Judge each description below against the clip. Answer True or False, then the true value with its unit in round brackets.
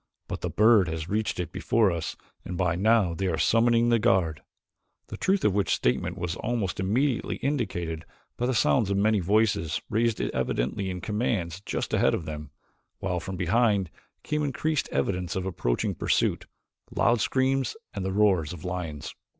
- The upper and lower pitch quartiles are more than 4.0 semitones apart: True (5.0 semitones)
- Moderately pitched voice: False (95 Hz)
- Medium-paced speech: True (165 wpm)